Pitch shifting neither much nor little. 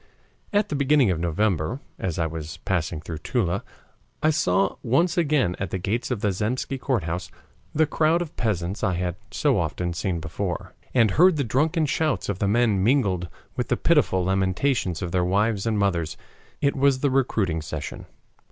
No: wide, 7.2 semitones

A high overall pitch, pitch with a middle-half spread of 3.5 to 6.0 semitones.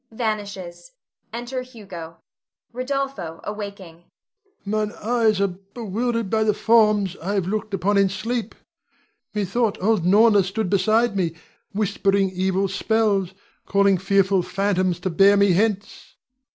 No: high, 200 Hz; narrow, 2.6 semitones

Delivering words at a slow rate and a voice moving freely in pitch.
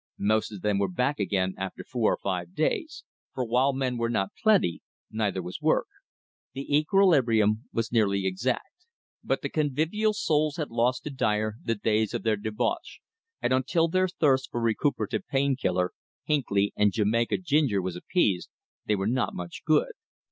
No: average, 170 wpm; wide, 6.1 semitones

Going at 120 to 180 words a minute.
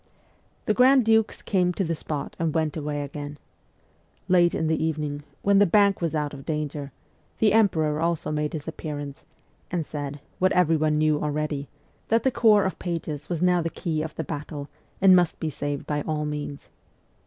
No: average, 190 wpm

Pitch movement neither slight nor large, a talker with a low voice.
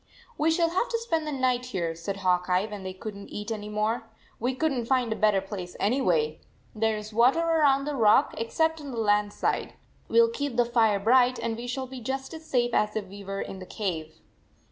No: average, 4.7 semitones; high, 230 Hz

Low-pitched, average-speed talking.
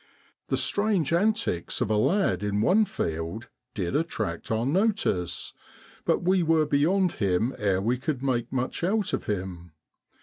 Yes: low, 125 Hz; average, 155 wpm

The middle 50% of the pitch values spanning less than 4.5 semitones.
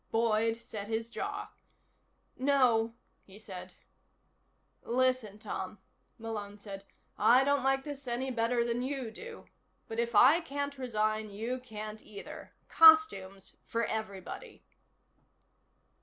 Yes: average, 3.4 semitones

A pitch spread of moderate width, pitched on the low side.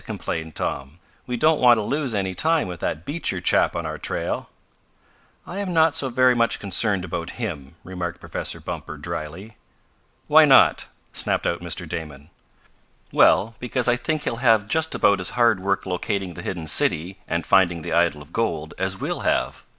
No: wide, 6.1 semitones; very low, 95 Hz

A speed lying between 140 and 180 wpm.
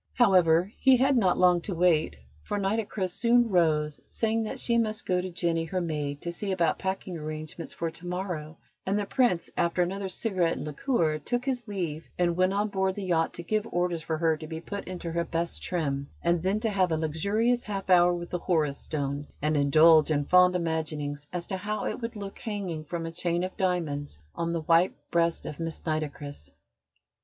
No: fast, 205 wpm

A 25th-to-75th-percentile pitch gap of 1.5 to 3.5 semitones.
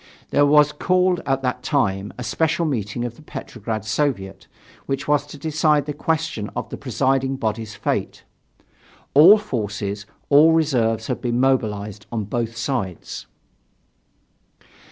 No: wide, 5.4 semitones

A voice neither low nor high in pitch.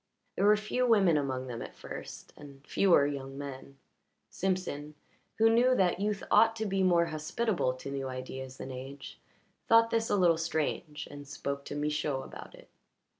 Yes: medium, 150 Hz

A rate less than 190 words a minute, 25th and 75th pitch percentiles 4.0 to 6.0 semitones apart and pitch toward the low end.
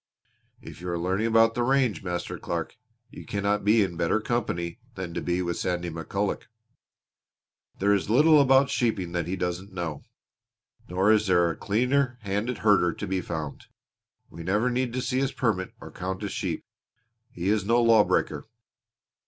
Yes: average, 170 wpm; average, 4.7 semitones; low, 100 Hz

